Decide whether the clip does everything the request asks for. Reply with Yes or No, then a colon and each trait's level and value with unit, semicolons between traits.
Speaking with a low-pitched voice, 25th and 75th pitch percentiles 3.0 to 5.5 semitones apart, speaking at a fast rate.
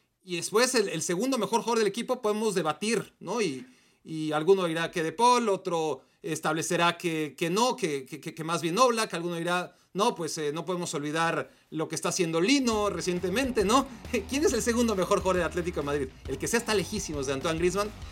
No: medium, 180 Hz; average, 5.0 semitones; fast, 210 wpm